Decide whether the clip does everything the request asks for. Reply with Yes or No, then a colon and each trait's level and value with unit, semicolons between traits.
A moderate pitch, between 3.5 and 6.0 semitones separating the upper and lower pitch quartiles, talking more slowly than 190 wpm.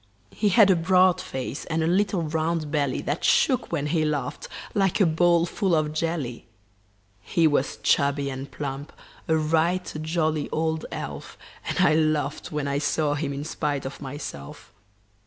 No: medium, 155 Hz; average, 2.7 semitones; average, 165 wpm